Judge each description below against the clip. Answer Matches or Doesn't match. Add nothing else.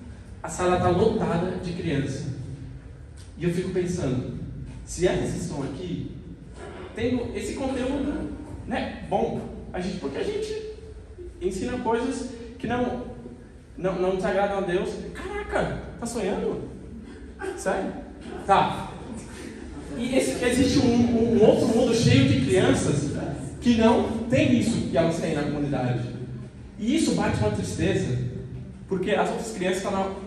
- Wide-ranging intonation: Matches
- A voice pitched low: Doesn't match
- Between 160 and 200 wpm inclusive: Doesn't match